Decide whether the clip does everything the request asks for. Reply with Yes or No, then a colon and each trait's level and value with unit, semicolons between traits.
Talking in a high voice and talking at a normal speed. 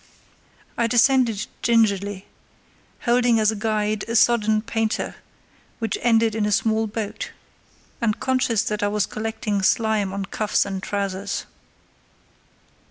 No: high, 220 Hz; slow, 125 wpm